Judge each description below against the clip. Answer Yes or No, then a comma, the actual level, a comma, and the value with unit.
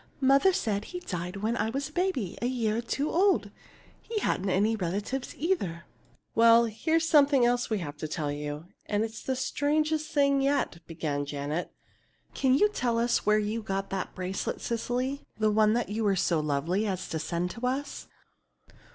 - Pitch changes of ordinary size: No, wide, 6.8 semitones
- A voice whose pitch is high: Yes, high, 225 Hz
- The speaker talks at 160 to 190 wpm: Yes, average, 180 wpm